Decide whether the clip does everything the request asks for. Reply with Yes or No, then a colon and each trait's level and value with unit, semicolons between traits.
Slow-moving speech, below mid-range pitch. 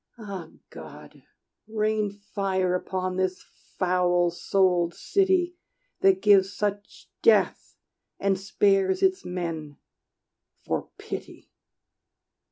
No: slow, 90 wpm; high, 190 Hz